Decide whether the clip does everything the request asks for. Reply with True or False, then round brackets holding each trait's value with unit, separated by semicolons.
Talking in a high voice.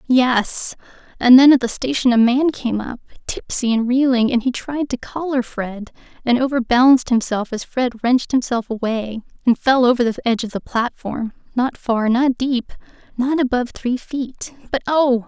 True (245 Hz)